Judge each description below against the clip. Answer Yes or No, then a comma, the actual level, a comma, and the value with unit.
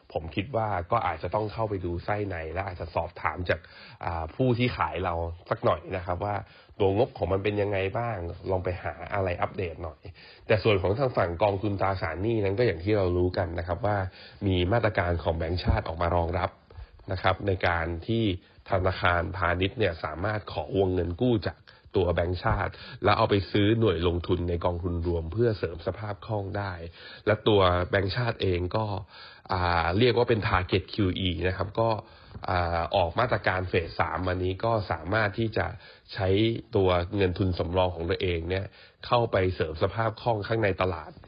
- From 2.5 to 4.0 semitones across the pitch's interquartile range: Yes, average, 3.0 semitones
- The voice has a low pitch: Yes, very low, 95 Hz